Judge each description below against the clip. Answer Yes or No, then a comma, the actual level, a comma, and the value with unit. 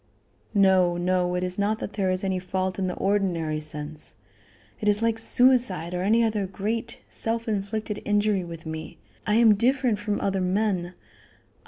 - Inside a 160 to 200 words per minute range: Yes, average, 170 wpm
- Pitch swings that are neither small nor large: Yes, average, 3.0 semitones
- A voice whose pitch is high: Yes, high, 195 Hz